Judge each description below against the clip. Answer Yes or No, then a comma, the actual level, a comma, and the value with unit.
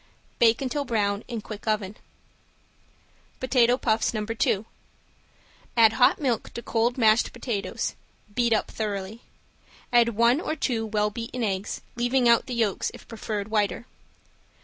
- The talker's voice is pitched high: Yes, high, 230 Hz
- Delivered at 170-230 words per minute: No, average, 140 wpm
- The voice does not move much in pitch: Yes, narrow, 2.2 semitones